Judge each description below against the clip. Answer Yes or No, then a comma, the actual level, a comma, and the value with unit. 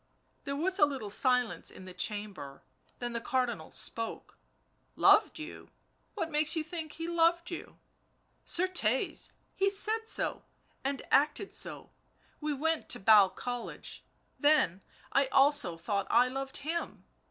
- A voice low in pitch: No, very high, 275 Hz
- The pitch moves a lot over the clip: Yes, wide, 6.3 semitones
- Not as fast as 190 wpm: Yes, average, 155 wpm